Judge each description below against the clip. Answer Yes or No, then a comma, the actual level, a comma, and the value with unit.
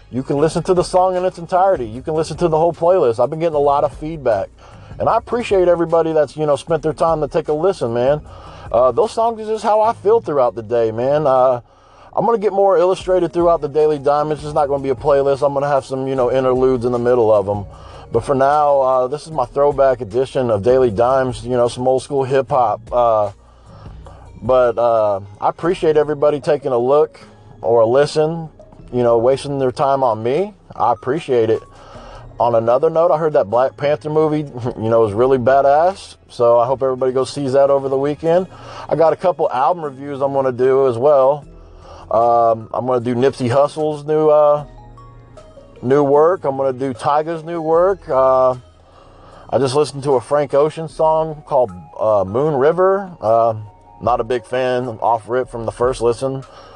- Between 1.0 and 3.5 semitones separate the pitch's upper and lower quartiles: No, average, 4.3 semitones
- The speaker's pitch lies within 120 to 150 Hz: Yes, low, 135 Hz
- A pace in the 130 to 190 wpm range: No, fast, 205 wpm